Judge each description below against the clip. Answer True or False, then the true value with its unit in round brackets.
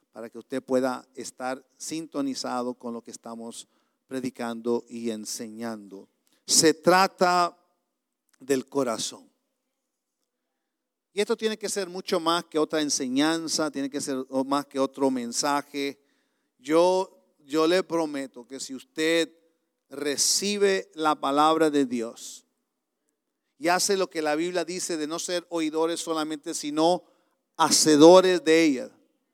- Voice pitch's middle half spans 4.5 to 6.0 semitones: True (4.9 semitones)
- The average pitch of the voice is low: False (155 Hz)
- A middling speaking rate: False (125 wpm)